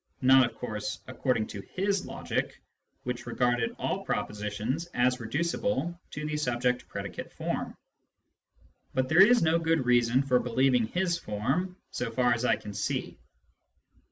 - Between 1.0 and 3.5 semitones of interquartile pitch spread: No, wide, 5.5 semitones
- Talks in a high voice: No, low, 125 Hz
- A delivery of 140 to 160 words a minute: Yes, average, 145 wpm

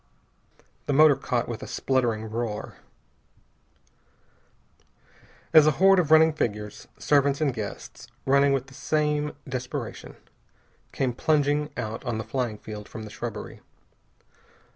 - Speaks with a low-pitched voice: Yes, low, 130 Hz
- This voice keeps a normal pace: No, slow, 125 wpm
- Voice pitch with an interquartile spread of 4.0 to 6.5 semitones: Yes, average, 4.9 semitones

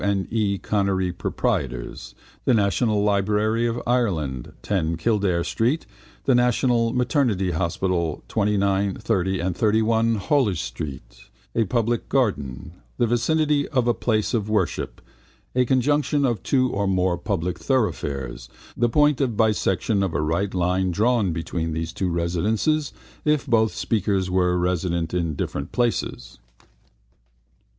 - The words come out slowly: Yes, slow, 130 wpm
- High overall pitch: No, low, 100 Hz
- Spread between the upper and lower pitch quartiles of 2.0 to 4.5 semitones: No, average, 5.2 semitones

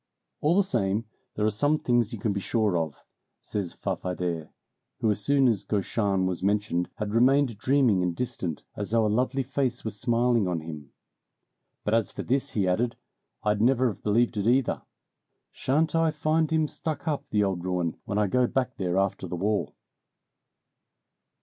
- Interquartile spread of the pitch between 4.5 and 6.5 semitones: Yes, average, 5.1 semitones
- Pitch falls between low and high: No, low, 110 Hz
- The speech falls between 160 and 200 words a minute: Yes, average, 180 wpm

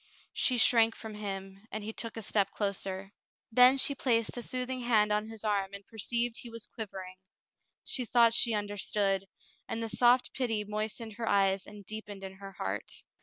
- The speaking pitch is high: Yes, high, 215 Hz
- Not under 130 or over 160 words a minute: No, average, 180 wpm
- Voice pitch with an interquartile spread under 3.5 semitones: Yes, average, 2.7 semitones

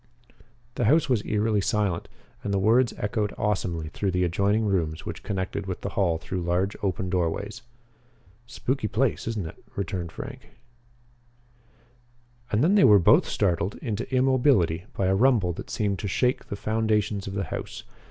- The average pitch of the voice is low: Yes, low, 100 Hz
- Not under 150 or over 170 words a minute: Yes, average, 160 wpm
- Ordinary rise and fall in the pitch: Yes, average, 3.4 semitones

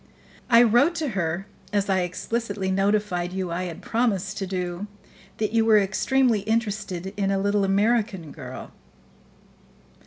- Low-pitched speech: No, high, 200 Hz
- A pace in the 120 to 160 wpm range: Yes, average, 145 wpm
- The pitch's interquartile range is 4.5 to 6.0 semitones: No, average, 2.9 semitones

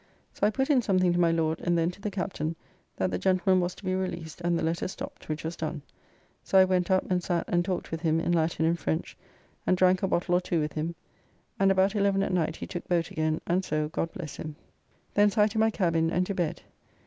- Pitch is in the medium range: Yes, medium, 175 Hz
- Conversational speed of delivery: No, fast, 250 wpm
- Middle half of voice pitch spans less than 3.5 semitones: Yes, narrow, 2.5 semitones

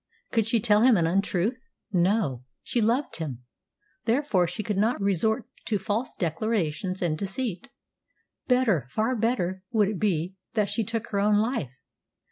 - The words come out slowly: No, average, 155 wpm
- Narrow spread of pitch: No, average, 4.2 semitones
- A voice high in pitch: Yes, high, 210 Hz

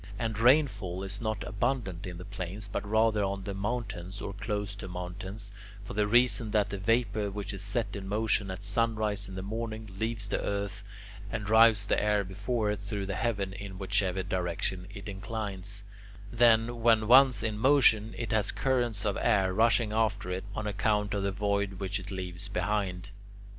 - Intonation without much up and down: Yes, narrow, 2.2 semitones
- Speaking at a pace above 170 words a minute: Yes, average, 185 wpm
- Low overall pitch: Yes, low, 105 Hz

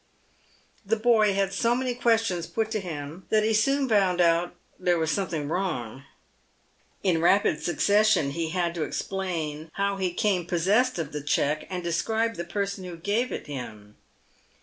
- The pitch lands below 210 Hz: Yes, medium, 185 Hz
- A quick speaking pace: No, average, 165 wpm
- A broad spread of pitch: No, average, 4.6 semitones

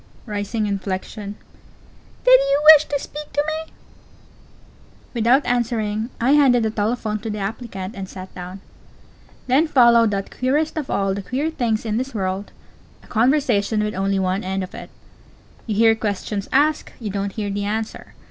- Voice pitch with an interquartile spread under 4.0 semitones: No, average, 4.3 semitones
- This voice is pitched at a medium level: No, high, 220 Hz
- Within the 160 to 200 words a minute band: Yes, average, 165 wpm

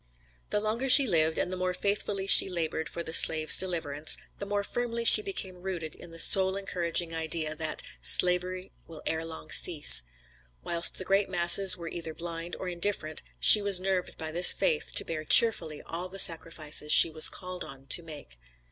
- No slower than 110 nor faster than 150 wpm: No, average, 185 wpm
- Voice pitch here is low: No, medium, 175 Hz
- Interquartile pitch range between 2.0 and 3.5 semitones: Yes, average, 3.1 semitones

